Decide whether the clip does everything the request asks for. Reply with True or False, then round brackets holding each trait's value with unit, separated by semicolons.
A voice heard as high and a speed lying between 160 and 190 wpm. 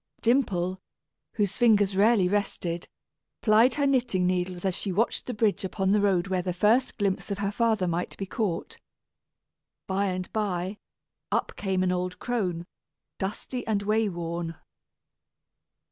False (195 Hz; 145 wpm)